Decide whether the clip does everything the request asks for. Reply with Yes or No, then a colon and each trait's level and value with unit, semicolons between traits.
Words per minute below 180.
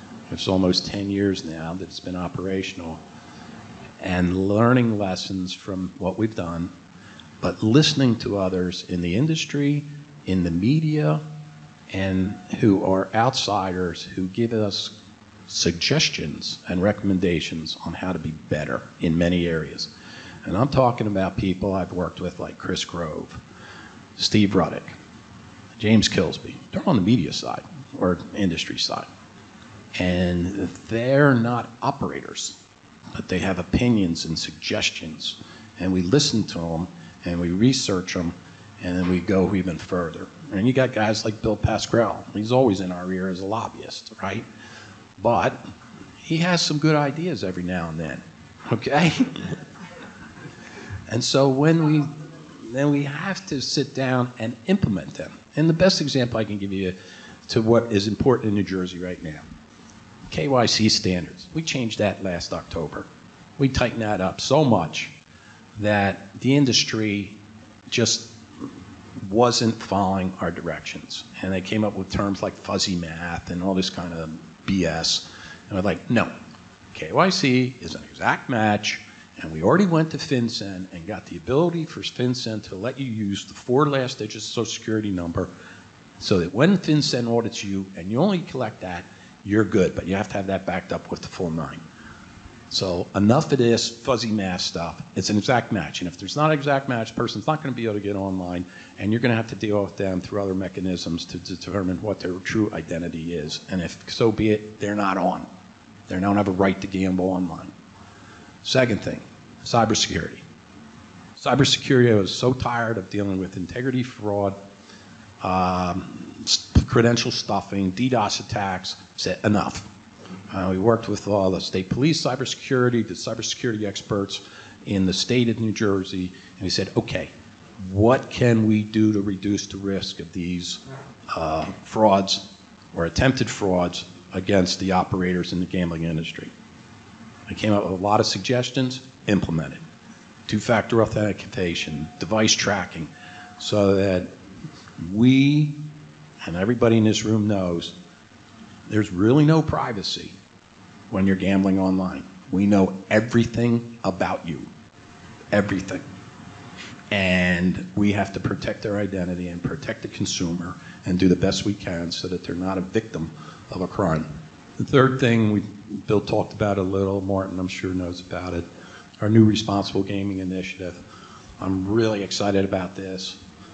Yes: average, 160 wpm